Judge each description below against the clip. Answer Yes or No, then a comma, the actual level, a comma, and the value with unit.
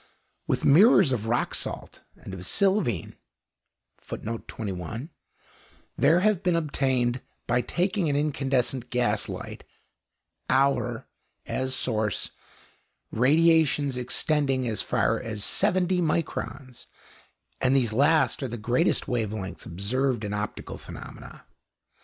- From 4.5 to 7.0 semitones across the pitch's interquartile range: Yes, average, 4.8 semitones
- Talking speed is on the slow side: Yes, slow, 110 wpm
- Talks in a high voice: No, low, 130 Hz